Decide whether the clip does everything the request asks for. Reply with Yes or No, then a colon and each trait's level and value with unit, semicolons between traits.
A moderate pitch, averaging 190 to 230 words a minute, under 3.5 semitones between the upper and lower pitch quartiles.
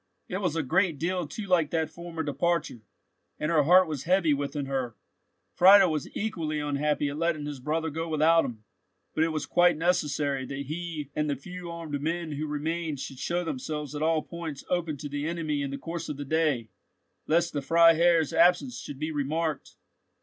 Yes: medium, 155 Hz; average, 195 wpm; average, 2.7 semitones